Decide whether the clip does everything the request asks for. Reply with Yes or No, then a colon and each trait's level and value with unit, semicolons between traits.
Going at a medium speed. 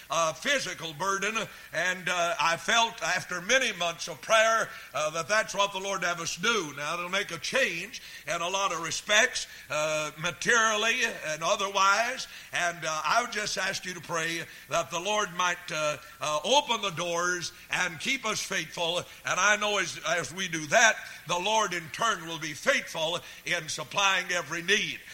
Yes: average, 180 wpm